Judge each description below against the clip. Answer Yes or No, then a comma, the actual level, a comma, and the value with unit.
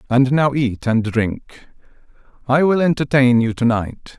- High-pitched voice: No, low, 130 Hz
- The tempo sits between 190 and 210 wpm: No, average, 160 wpm